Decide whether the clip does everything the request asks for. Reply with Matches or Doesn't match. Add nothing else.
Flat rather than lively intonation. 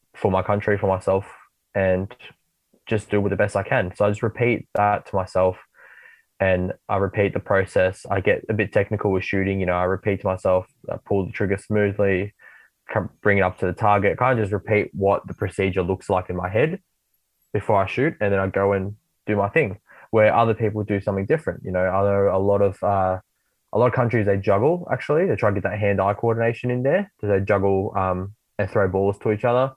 Matches